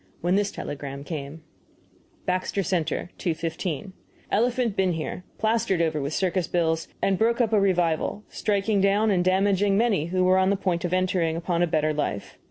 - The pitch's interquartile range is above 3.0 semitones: Yes, average, 3.4 semitones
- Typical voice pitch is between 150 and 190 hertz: Yes, medium, 185 Hz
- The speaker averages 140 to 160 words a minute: No, average, 180 wpm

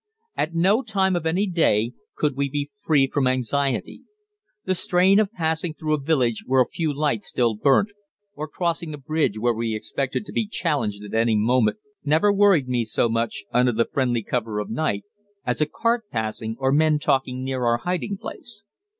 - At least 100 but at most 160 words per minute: No, average, 190 wpm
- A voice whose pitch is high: No, medium, 140 Hz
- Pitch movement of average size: No, wide, 6.0 semitones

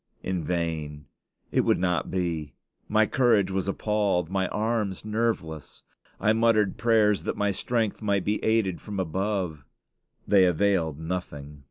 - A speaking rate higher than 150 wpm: No, average, 140 wpm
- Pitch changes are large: No, average, 4.0 semitones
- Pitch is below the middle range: Yes, very low, 95 Hz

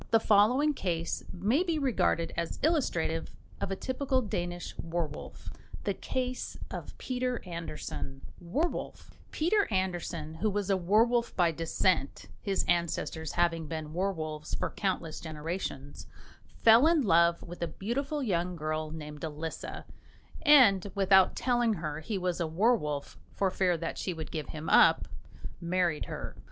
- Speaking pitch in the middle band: Yes, medium, 180 Hz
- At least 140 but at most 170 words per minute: Yes, average, 145 wpm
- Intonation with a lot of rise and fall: Yes, wide, 5.8 semitones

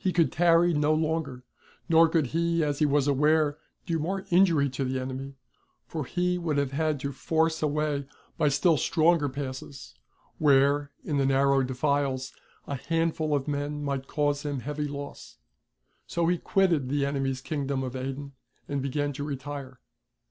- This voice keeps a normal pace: Yes, average, 165 wpm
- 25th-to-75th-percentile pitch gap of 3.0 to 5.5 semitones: No, narrow, 2.6 semitones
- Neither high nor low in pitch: Yes, medium, 145 Hz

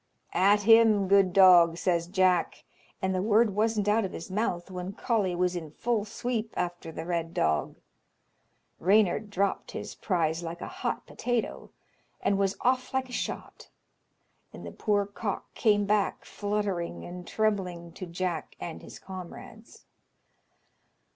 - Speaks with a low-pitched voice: No, high, 195 Hz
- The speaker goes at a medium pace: Yes, average, 145 wpm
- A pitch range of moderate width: Yes, average, 3.3 semitones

